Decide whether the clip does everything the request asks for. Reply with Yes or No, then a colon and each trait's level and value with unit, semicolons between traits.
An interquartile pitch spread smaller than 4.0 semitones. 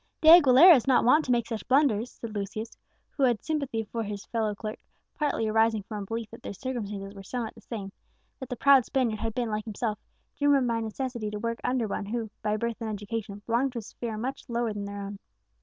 Yes: average, 3.0 semitones